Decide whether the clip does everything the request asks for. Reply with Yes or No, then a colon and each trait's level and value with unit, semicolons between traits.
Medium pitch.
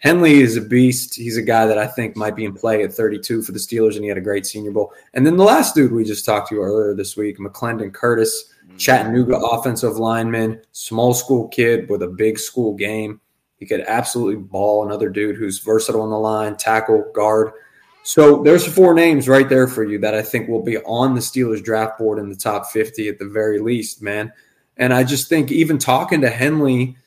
No: low, 110 Hz